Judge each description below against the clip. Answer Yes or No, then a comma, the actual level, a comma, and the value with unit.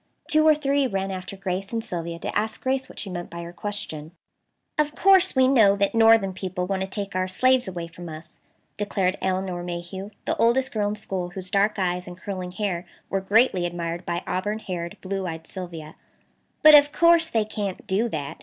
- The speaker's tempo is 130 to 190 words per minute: No, average, 200 wpm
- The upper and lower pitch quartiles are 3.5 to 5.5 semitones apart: Yes, average, 3.8 semitones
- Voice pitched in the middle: No, high, 195 Hz